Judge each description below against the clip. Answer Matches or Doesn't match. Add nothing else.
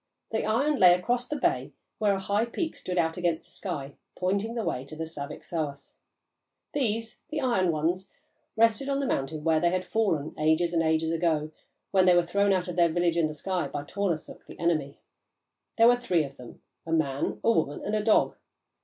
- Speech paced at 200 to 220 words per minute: Matches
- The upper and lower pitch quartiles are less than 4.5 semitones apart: Doesn't match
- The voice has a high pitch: Doesn't match